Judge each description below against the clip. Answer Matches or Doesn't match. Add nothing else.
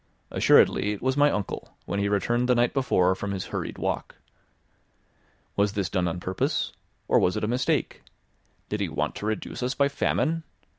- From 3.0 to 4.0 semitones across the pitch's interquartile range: Doesn't match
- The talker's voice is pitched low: Matches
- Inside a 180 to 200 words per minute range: Matches